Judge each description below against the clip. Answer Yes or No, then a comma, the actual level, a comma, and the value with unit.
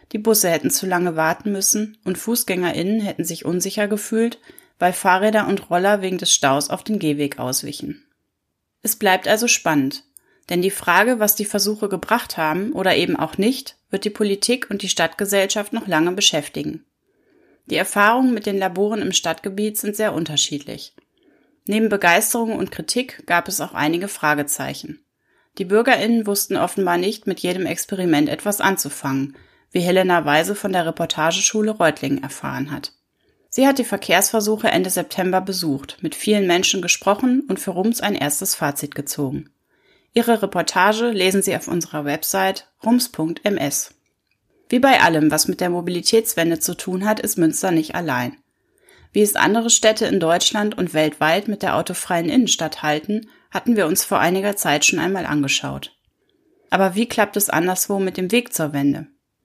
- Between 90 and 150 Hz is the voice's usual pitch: No, high, 190 Hz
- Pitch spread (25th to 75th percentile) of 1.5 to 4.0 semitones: No, average, 4.5 semitones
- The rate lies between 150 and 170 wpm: Yes, average, 160 wpm